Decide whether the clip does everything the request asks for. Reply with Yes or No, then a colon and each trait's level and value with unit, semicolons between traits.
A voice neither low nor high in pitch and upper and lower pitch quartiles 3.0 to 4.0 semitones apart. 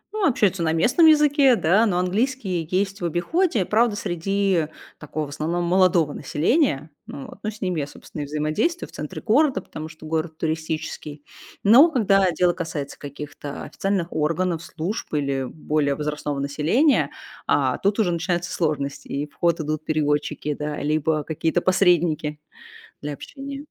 No: medium, 170 Hz; average, 4.9 semitones